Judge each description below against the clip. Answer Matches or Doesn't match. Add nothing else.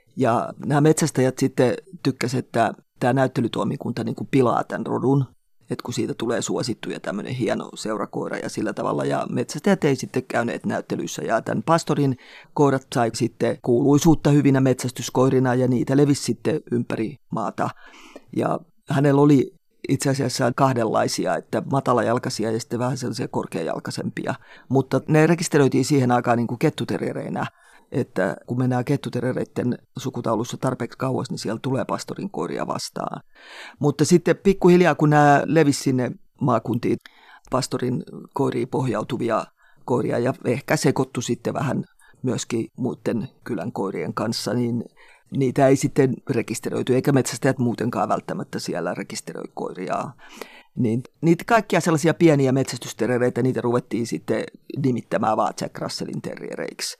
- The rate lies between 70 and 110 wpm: Doesn't match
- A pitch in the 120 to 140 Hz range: Matches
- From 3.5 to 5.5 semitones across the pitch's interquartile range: Doesn't match